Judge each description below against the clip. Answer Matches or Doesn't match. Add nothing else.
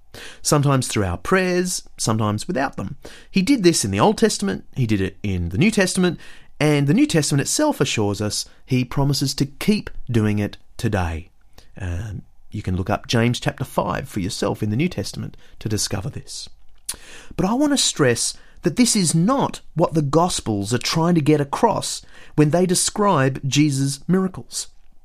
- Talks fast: Doesn't match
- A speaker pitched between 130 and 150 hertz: Matches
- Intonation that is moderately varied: Doesn't match